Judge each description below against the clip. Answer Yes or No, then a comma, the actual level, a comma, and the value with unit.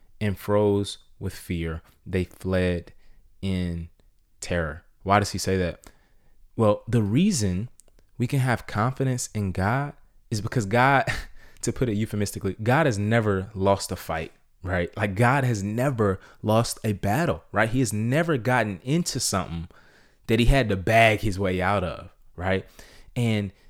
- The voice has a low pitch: Yes, low, 105 Hz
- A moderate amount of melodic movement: Yes, average, 4.1 semitones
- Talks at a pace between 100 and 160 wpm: Yes, average, 155 wpm